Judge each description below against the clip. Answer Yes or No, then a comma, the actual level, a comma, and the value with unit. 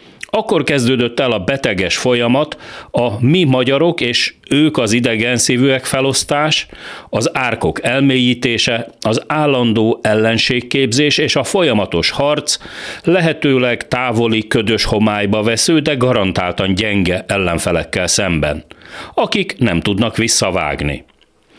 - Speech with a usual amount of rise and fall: Yes, average, 4.0 semitones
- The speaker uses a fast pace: No, average, 110 wpm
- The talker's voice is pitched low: Yes, low, 120 Hz